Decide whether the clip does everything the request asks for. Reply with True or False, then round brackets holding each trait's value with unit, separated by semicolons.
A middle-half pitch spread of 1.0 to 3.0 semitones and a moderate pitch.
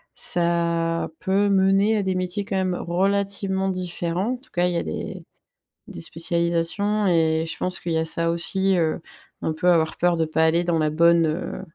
True (2.4 semitones; 175 Hz)